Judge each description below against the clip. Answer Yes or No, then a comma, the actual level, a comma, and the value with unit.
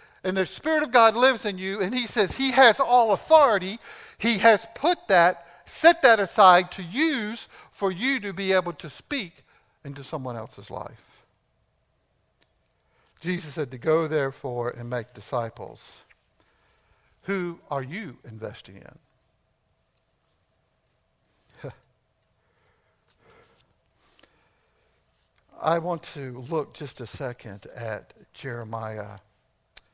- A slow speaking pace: Yes, slow, 115 wpm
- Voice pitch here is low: No, medium, 165 Hz